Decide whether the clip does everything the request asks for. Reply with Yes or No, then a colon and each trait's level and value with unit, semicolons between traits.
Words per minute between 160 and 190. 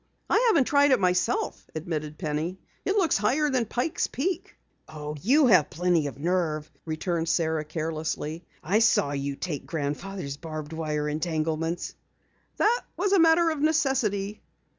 No: average, 145 wpm